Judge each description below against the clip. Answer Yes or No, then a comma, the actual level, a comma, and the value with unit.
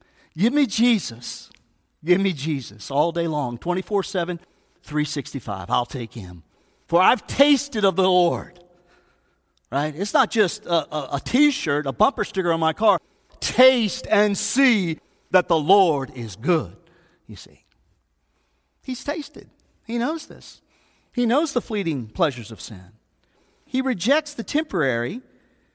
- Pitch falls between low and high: Yes, medium, 175 Hz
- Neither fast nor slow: Yes, average, 145 wpm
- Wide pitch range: Yes, wide, 8.8 semitones